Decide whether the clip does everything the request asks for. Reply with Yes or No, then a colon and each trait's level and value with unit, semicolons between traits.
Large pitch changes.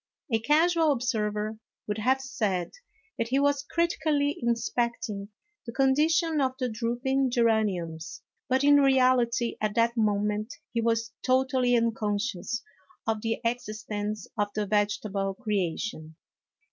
No: average, 3.9 semitones